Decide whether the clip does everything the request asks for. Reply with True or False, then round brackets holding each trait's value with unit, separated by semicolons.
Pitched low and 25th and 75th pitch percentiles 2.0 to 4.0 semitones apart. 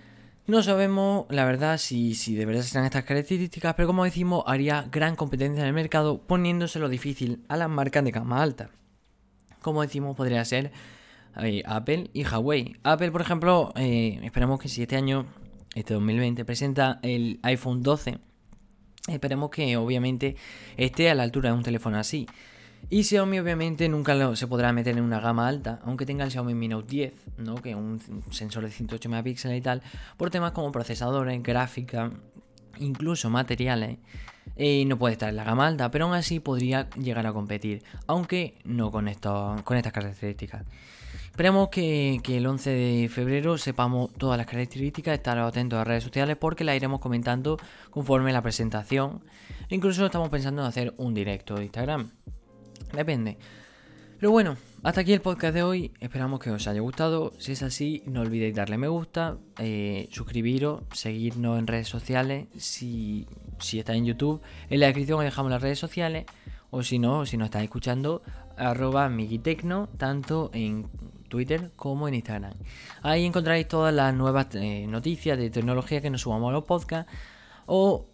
False (125 Hz; 4.6 semitones)